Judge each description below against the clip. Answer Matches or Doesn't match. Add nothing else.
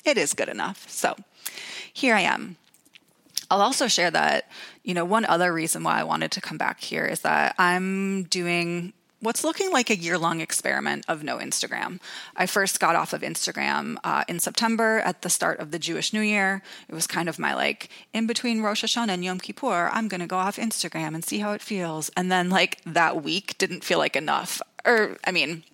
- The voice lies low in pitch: Doesn't match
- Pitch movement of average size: Matches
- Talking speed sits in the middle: Doesn't match